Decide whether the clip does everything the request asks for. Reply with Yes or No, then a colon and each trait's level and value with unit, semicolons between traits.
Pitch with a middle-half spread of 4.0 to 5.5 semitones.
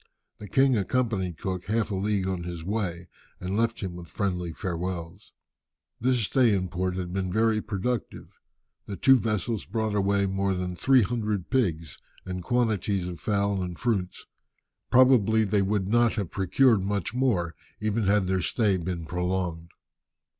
No: average, 3.4 semitones